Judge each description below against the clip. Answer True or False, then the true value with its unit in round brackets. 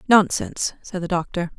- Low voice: False (185 Hz)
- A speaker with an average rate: True (150 wpm)